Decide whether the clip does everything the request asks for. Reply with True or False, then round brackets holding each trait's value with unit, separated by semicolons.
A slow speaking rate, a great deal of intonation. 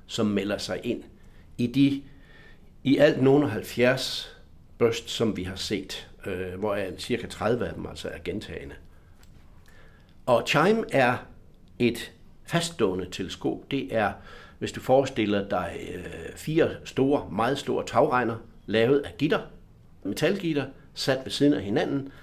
True (140 wpm; 5.7 semitones)